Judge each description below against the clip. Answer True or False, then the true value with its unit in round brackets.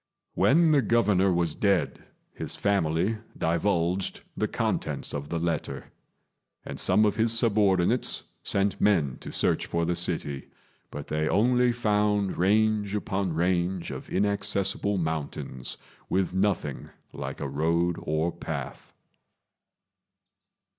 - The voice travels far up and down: False (3.8 semitones)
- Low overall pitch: True (95 Hz)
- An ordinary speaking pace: False (120 wpm)